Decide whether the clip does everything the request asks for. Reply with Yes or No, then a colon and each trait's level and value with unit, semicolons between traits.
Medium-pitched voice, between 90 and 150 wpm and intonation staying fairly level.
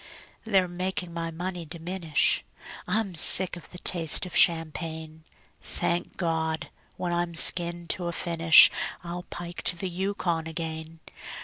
Yes: medium, 170 Hz; slow, 135 wpm; narrow, 1.6 semitones